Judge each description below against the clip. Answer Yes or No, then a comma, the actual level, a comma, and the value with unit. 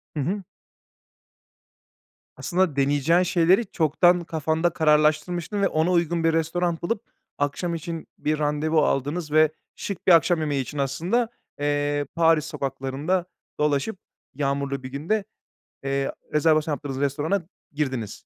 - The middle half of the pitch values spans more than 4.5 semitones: No, average, 3.1 semitones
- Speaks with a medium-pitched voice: Yes, medium, 155 Hz